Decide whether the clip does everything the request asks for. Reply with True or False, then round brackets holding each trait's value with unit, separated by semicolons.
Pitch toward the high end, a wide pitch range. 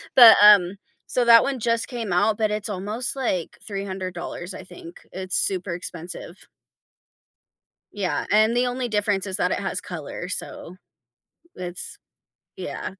False (200 Hz; 3.6 semitones)